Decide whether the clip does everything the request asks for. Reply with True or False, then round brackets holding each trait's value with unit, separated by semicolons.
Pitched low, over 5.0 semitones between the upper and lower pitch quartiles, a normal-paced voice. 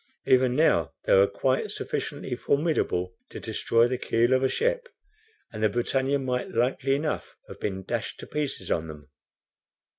True (125 Hz; 5.5 semitones; 160 wpm)